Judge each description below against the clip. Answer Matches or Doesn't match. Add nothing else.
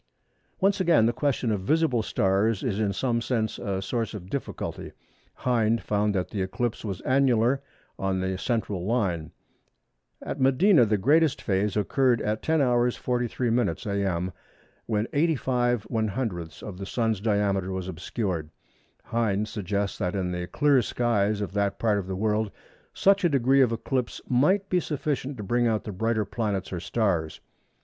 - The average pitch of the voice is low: Matches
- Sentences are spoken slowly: Doesn't match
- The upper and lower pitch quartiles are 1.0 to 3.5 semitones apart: Doesn't match